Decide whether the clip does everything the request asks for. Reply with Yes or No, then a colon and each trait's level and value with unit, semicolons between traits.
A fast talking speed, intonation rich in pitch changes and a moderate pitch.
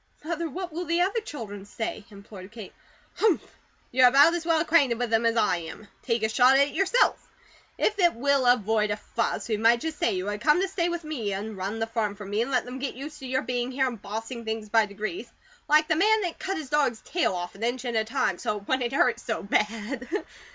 No: fast, 250 wpm; wide, 6.0 semitones; high, 245 Hz